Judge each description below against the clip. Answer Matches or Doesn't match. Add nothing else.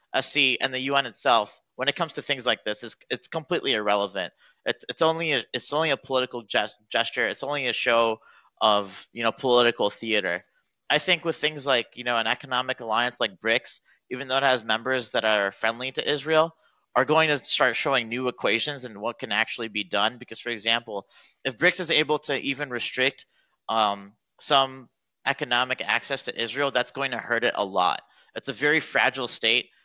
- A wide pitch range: Doesn't match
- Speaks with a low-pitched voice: Matches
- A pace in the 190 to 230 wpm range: Matches